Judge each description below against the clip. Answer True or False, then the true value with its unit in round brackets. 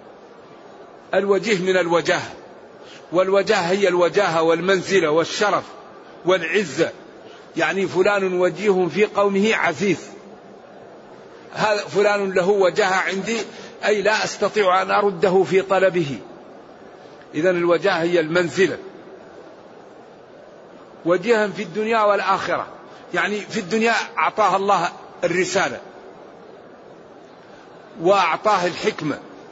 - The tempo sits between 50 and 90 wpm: True (85 wpm)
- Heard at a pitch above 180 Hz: True (190 Hz)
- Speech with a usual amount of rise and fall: False (2.3 semitones)